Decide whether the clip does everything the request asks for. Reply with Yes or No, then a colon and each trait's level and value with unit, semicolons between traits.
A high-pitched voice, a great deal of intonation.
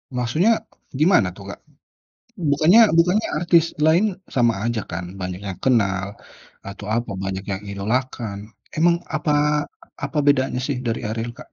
No: low, 125 Hz; wide, 7.7 semitones